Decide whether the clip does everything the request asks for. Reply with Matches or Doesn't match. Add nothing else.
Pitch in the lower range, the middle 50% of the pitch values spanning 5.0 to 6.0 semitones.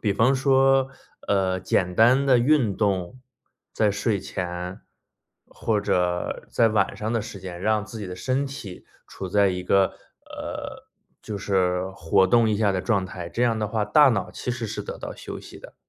Doesn't match